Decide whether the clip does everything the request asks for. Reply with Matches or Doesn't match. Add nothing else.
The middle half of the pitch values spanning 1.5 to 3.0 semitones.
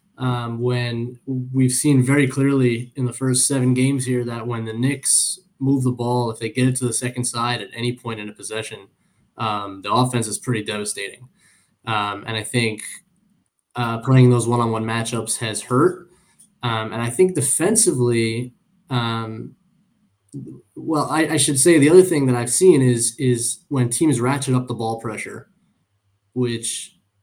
Matches